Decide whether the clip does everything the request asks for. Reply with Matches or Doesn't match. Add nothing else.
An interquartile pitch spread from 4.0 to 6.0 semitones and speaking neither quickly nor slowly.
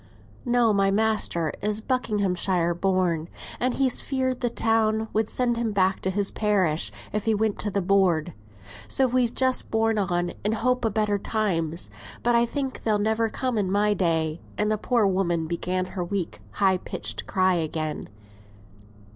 Doesn't match